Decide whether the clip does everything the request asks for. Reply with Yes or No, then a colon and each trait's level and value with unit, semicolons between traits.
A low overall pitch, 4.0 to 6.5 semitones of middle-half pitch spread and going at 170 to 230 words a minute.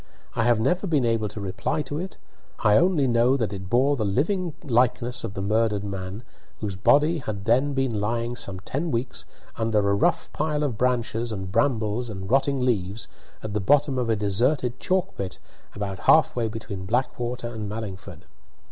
Yes: low, 115 Hz; average, 4.5 semitones; average, 185 wpm